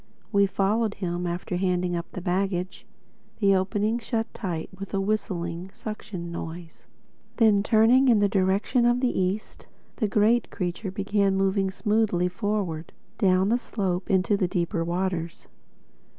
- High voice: Yes, high, 195 Hz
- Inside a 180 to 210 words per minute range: No, average, 145 wpm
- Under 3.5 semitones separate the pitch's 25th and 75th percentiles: Yes, average, 3.0 semitones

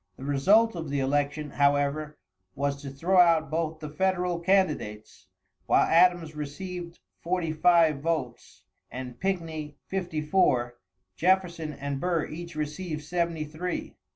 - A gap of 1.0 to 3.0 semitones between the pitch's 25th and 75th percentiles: No, average, 3.6 semitones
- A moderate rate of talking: No, slow, 130 wpm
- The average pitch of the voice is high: No, medium, 160 Hz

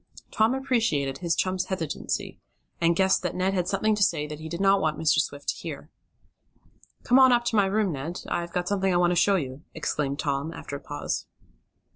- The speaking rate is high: Yes, fast, 210 wpm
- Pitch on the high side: No, medium, 180 Hz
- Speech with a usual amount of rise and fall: Yes, average, 4.7 semitones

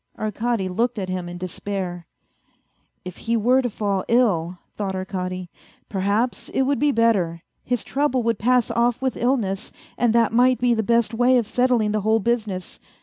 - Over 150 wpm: Yes, average, 185 wpm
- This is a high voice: Yes, high, 225 Hz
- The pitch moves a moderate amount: Yes, average, 4.2 semitones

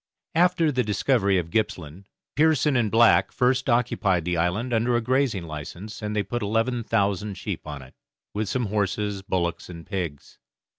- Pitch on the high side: No, low, 105 Hz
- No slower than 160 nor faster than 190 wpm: Yes, average, 165 wpm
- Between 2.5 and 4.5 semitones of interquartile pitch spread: No, average, 4.9 semitones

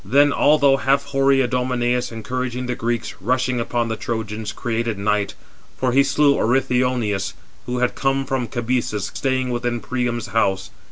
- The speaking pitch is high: No, low, 125 Hz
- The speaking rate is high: No, average, 150 wpm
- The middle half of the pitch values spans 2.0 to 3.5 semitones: Yes, narrow, 2.4 semitones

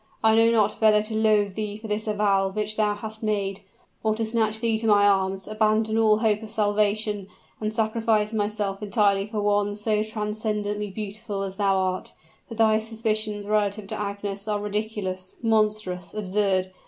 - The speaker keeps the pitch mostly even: Yes, narrow, 1.2 semitones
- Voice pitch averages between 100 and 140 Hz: No, high, 210 Hz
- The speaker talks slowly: No, average, 170 wpm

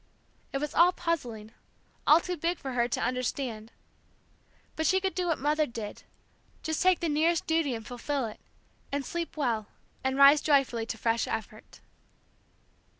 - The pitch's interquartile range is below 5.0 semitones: No, wide, 5.6 semitones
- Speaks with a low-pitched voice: No, very high, 280 Hz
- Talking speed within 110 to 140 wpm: No, average, 160 wpm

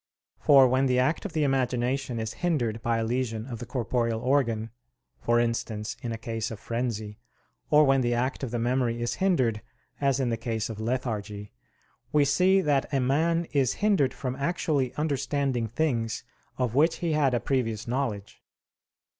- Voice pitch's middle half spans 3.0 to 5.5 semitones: Yes, average, 3.3 semitones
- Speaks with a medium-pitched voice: No, low, 125 Hz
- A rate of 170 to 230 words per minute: Yes, average, 175 wpm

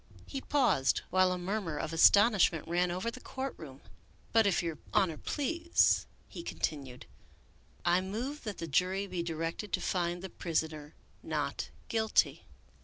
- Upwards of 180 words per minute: No, average, 160 wpm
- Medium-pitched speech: Yes, medium, 180 Hz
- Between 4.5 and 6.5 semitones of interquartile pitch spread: Yes, average, 5.1 semitones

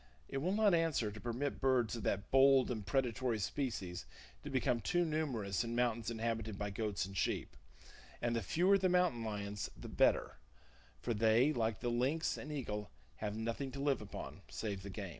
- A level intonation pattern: No, average, 4.5 semitones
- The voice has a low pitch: Yes, low, 120 Hz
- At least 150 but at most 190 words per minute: Yes, average, 185 wpm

